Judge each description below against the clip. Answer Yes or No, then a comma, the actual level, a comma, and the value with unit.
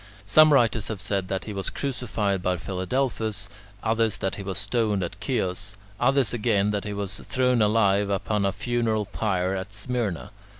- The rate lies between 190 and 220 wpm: No, average, 170 wpm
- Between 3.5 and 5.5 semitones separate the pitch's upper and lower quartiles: No, average, 2.8 semitones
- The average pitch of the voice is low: Yes, low, 105 Hz